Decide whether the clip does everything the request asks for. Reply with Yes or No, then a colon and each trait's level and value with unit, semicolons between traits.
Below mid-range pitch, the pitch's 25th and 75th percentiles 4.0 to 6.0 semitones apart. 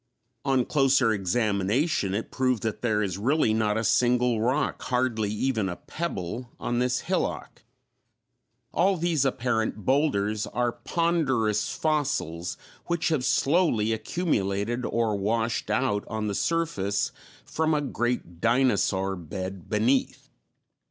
Yes: low, 115 Hz; average, 4.5 semitones